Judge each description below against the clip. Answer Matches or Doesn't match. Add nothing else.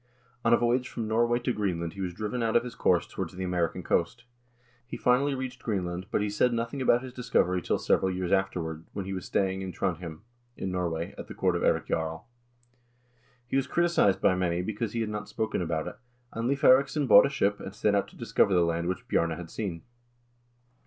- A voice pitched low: Matches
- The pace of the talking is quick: Matches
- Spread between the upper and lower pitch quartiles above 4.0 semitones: Matches